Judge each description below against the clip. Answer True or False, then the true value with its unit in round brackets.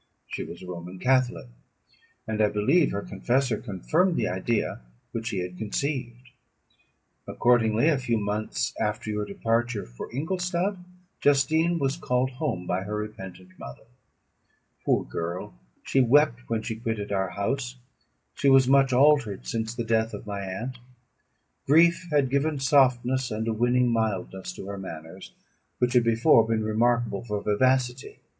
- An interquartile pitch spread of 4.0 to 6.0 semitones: True (4.3 semitones)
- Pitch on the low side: True (115 Hz)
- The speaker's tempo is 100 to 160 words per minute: True (150 wpm)